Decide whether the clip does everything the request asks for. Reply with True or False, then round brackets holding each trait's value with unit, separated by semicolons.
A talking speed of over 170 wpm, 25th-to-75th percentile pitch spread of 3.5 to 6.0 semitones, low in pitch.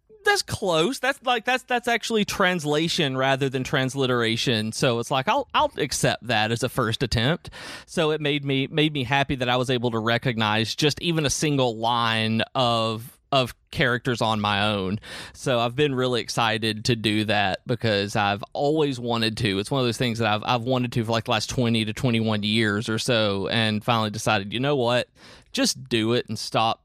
True (200 wpm; 3.9 semitones; 125 Hz)